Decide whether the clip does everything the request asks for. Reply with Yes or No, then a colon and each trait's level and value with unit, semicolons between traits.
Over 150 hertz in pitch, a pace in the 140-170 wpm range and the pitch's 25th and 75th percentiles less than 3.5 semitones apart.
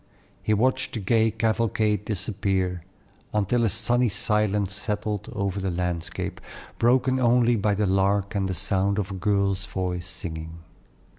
No: low, 100 Hz; average, 145 wpm; narrow, 2.6 semitones